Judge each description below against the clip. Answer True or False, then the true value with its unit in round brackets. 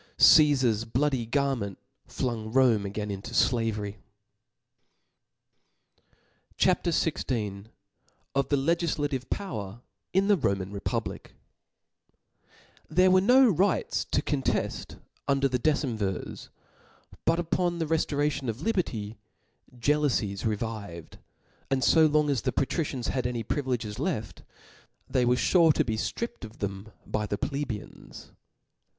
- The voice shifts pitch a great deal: True (5.7 semitones)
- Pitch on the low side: True (130 Hz)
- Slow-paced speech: True (120 wpm)